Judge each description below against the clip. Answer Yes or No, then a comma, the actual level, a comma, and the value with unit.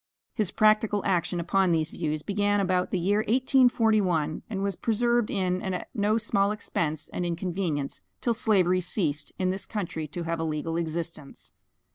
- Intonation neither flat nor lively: Yes, average, 3.9 semitones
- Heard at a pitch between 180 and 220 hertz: Yes, medium, 185 Hz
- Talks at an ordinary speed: Yes, average, 160 wpm